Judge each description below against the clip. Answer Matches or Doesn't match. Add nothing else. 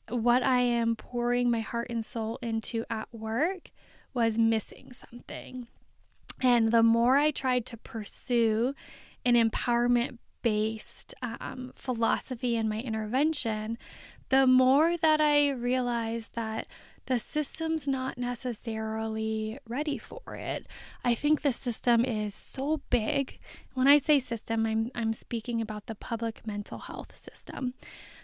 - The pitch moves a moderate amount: Doesn't match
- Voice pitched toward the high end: Matches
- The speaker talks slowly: Matches